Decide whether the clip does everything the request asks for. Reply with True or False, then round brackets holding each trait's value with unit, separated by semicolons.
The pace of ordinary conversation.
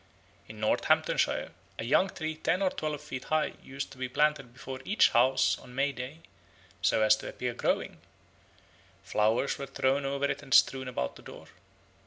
True (175 wpm)